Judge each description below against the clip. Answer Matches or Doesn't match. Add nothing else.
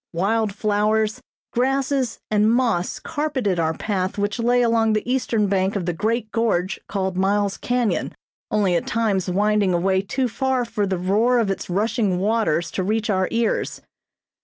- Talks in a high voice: Matches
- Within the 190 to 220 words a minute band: Doesn't match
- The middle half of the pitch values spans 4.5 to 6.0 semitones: Doesn't match